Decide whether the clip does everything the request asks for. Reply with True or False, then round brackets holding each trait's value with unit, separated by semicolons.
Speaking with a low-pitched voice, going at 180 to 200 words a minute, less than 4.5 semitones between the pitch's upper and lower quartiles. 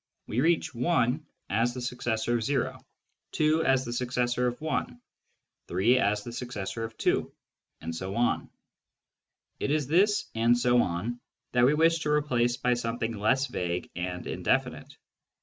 False (120 Hz; 165 wpm; 3.0 semitones)